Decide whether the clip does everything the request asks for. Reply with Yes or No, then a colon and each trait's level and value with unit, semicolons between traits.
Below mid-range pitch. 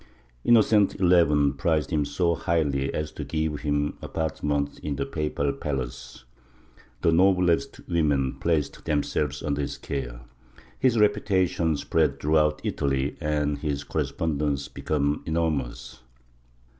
Yes: very low, 75 Hz